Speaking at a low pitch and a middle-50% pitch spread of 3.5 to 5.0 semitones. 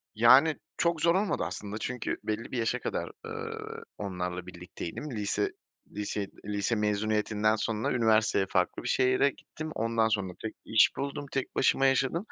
Yes: low, 110 Hz; average, 4.0 semitones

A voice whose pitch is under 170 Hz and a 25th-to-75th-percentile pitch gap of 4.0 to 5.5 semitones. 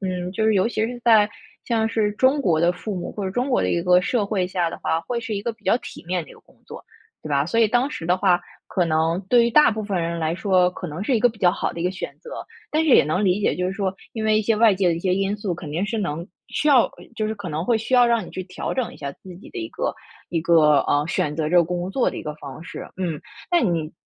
No: high, 190 Hz; average, 4.6 semitones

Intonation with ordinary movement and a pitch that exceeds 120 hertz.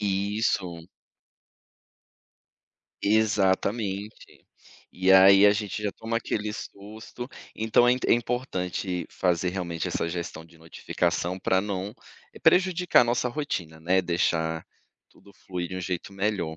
No: average, 3.5 semitones; very low, 95 Hz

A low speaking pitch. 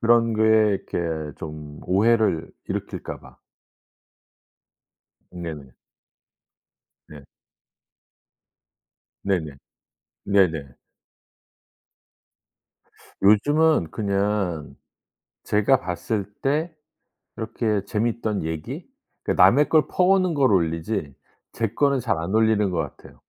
Yes: low, 105 Hz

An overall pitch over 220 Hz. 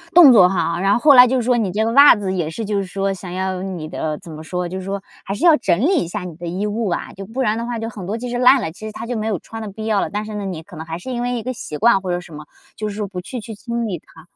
No: high, 200 Hz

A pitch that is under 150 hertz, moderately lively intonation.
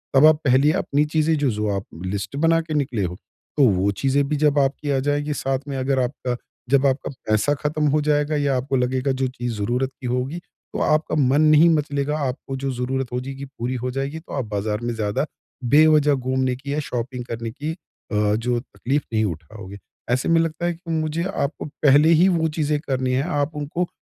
Yes: low, 135 Hz; average, 3.3 semitones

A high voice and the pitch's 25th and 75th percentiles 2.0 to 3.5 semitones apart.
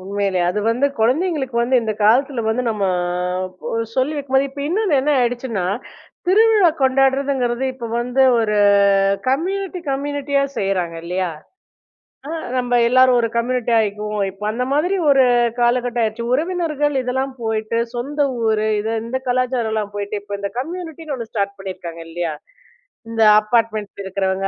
No: high, 245 Hz; average, 4.7 semitones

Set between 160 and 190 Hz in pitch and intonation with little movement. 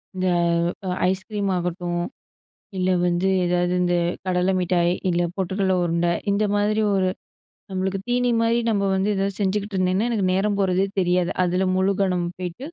Yes: medium, 185 Hz; narrow, 1.9 semitones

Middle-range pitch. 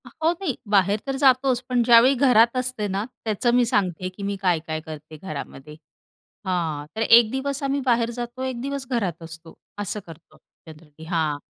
No: high, 215 Hz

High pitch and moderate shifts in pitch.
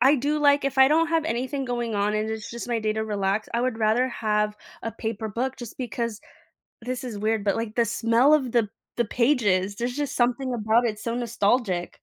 Yes: high, 235 Hz; average, 3.0 semitones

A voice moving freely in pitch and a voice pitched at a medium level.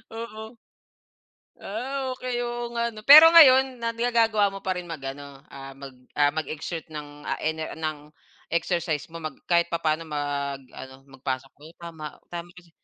Yes: wide, 6.8 semitones; medium, 165 Hz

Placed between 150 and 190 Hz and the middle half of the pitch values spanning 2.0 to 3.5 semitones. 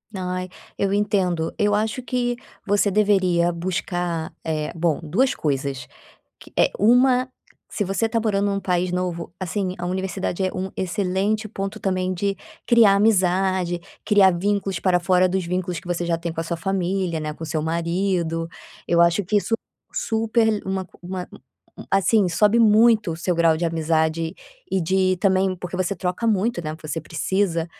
Yes: medium, 185 Hz; average, 3.0 semitones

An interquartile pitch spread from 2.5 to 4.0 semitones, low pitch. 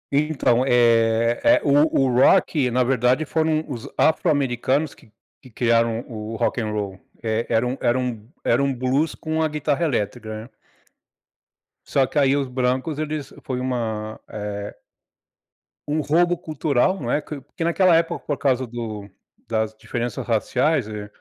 No: average, 4.6 semitones; low, 125 Hz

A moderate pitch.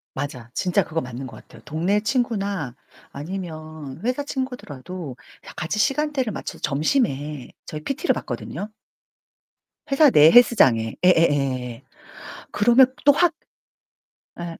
Yes: medium, 170 Hz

